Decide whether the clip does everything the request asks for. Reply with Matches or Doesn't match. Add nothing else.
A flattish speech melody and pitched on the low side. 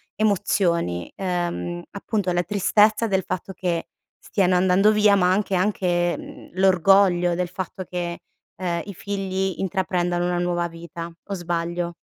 Doesn't match